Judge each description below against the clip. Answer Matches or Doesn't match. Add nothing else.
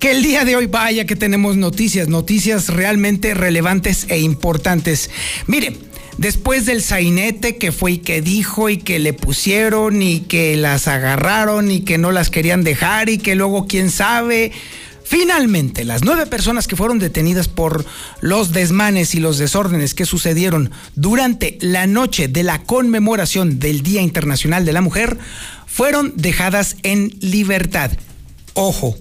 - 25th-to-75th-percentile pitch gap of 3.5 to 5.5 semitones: Matches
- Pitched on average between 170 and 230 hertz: Matches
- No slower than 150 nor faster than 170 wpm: Matches